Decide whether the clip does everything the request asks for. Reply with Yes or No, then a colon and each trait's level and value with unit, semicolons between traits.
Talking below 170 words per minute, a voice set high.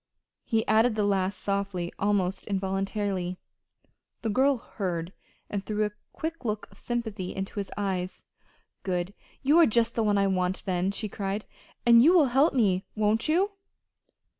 Yes: average, 160 wpm; high, 205 Hz